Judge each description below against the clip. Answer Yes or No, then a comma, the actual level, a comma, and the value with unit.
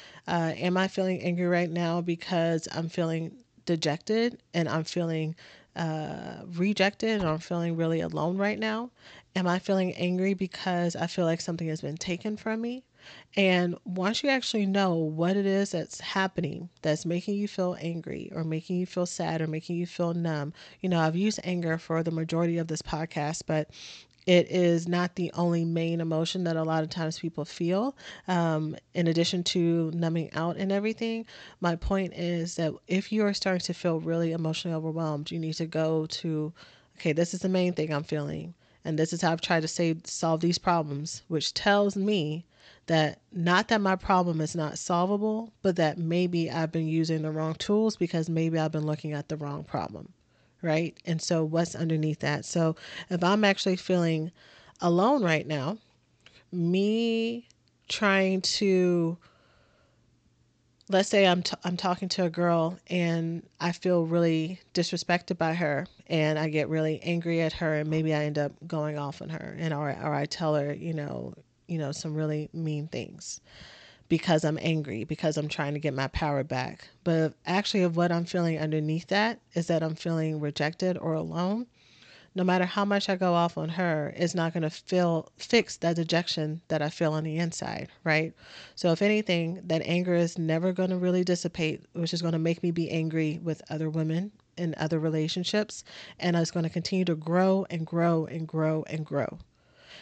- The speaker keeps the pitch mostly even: Yes, narrow, 2.3 semitones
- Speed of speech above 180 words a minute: Yes, average, 190 wpm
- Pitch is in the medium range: Yes, medium, 170 Hz